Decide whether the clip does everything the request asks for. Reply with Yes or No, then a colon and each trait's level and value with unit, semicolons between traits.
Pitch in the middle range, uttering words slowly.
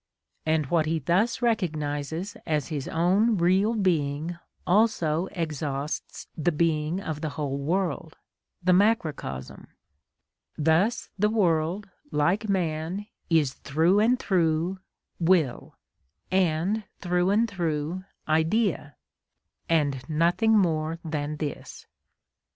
Yes: medium, 165 Hz; slow, 105 wpm